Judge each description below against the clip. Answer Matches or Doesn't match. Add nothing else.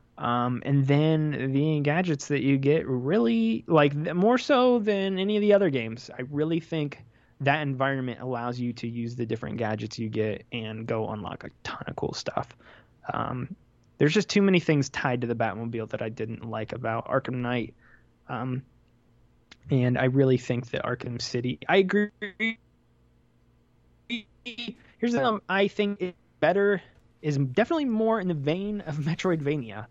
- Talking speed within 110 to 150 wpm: Doesn't match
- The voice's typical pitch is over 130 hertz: Matches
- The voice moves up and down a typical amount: Doesn't match